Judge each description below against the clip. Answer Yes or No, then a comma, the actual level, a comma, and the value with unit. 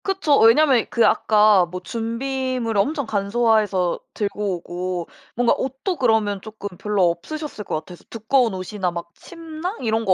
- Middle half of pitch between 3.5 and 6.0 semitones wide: Yes, wide, 5.4 semitones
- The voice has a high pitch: Yes, high, 220 Hz